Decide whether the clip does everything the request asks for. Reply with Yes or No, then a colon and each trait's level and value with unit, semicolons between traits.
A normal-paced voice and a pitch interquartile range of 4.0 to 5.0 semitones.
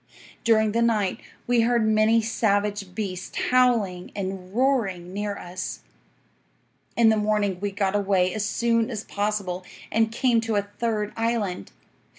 No: average, 145 wpm; average, 2.7 semitones